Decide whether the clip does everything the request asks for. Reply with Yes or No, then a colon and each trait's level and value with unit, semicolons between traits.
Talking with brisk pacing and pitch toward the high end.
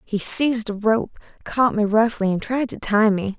Yes: fast, 215 wpm; high, 220 Hz